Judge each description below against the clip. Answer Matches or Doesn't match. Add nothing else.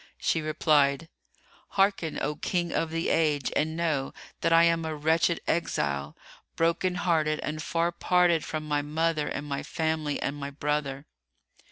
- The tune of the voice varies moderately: Doesn't match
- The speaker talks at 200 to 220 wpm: Doesn't match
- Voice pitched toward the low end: Doesn't match